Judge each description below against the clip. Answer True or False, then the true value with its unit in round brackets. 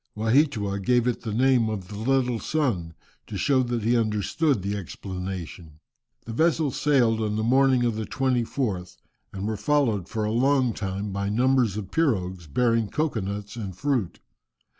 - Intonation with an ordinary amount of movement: True (4.5 semitones)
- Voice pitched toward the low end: True (110 Hz)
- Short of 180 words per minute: True (165 wpm)